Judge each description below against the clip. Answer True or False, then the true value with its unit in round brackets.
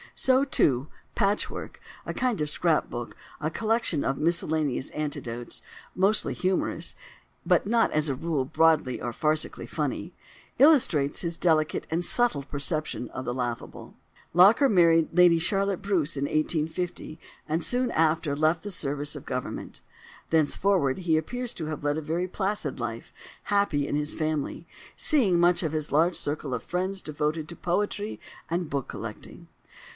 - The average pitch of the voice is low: False (160 Hz)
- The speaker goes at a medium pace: True (150 wpm)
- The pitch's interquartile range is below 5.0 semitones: True (4.1 semitones)